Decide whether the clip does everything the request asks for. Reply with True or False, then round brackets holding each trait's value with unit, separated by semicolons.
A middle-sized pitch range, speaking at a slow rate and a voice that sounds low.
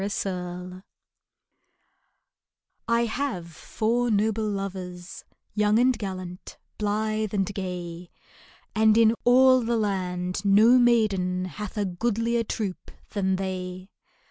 False (3.4 semitones; 110 wpm; 205 Hz)